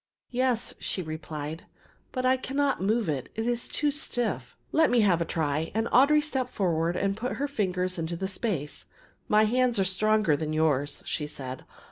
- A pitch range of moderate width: No, wide, 7.5 semitones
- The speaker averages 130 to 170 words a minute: No, average, 180 wpm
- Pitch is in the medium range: No, high, 195 Hz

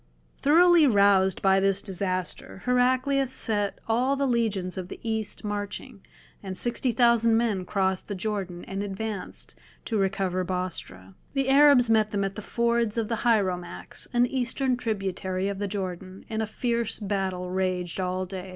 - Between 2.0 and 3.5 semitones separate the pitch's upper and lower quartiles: No, average, 3.9 semitones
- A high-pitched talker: Yes, high, 205 Hz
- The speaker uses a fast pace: No, average, 160 wpm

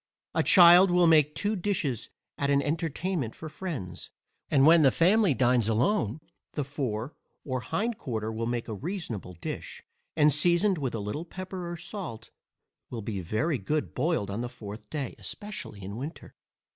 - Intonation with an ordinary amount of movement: No, wide, 7.2 semitones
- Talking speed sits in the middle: Yes, average, 170 wpm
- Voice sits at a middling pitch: Yes, medium, 145 Hz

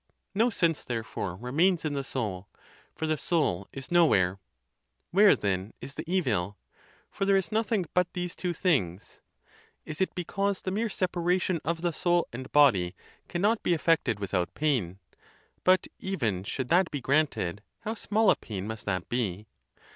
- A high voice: No, medium, 155 Hz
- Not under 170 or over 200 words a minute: No, average, 160 wpm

